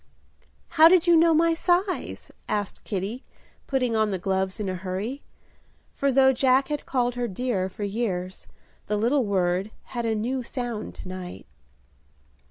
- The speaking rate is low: No, average, 160 wpm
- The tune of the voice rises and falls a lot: Yes, wide, 5.7 semitones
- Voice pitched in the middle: No, high, 235 Hz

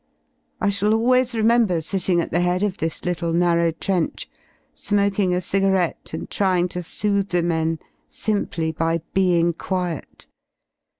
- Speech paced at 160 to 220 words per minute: No, slow, 135 wpm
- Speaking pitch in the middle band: Yes, medium, 180 Hz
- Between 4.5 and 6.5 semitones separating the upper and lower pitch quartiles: No, average, 3.0 semitones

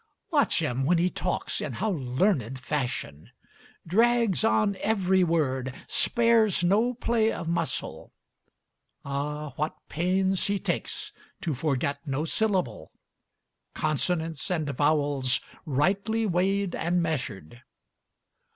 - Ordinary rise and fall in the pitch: No, wide, 5.9 semitones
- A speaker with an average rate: No, slow, 110 wpm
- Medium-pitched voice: Yes, medium, 170 Hz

